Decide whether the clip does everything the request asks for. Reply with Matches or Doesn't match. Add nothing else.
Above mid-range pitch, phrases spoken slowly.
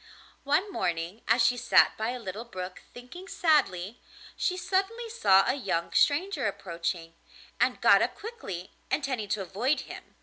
Doesn't match